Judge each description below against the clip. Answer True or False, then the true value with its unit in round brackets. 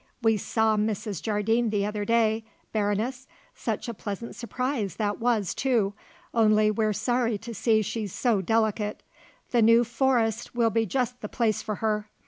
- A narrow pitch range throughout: True (1.9 semitones)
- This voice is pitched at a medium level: False (220 Hz)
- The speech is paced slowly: False (160 wpm)